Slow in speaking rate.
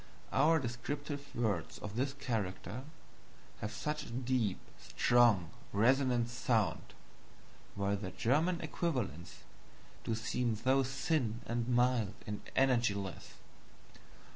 Yes: slow, 105 wpm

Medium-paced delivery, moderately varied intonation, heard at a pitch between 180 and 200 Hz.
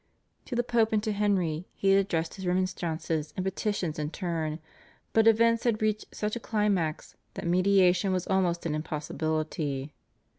Yes: average, 160 wpm; average, 4.6 semitones; medium, 185 Hz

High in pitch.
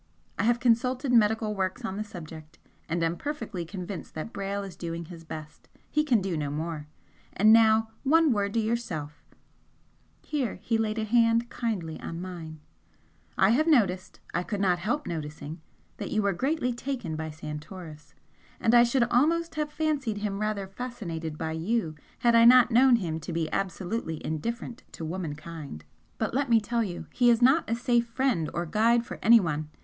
Yes: high, 210 Hz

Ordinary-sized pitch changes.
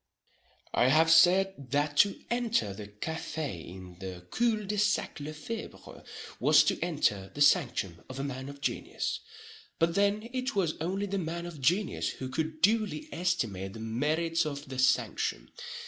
No: wide, 7.1 semitones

